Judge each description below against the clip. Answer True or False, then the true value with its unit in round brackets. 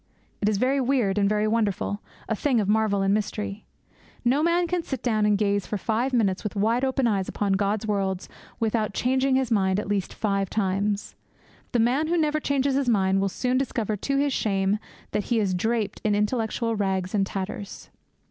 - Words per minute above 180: True (200 wpm)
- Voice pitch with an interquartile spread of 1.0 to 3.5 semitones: False (4.0 semitones)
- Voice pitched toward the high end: True (215 Hz)